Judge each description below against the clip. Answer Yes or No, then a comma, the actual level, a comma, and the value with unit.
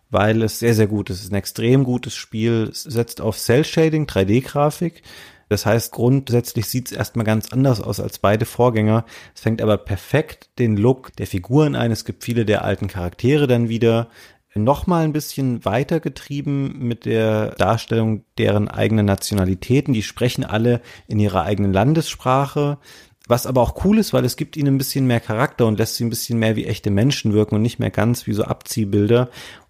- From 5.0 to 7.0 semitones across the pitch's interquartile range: No, average, 3.7 semitones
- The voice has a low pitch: Yes, low, 115 Hz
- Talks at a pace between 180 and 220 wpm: Yes, fast, 190 wpm